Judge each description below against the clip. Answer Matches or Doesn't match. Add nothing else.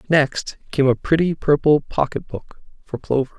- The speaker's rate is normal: Matches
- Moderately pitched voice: Matches